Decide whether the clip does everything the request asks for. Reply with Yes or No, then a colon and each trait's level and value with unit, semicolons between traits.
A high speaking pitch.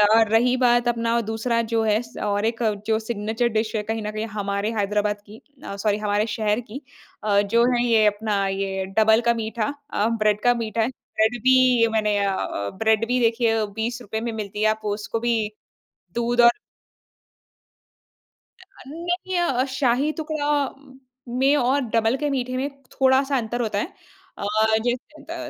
Yes: high, 225 Hz